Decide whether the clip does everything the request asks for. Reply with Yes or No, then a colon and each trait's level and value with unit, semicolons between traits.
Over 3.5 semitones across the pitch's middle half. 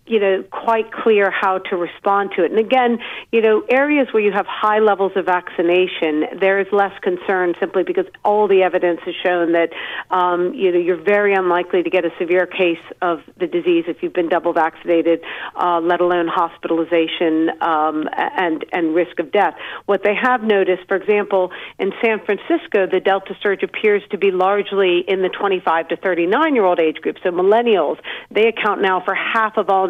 No: narrow, 2.6 semitones